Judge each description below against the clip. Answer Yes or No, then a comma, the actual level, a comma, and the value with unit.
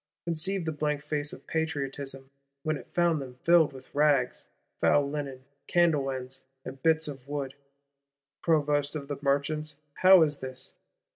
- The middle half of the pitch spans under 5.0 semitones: Yes, narrow, 2.5 semitones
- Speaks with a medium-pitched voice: Yes, medium, 145 Hz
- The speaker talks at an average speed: Yes, average, 150 wpm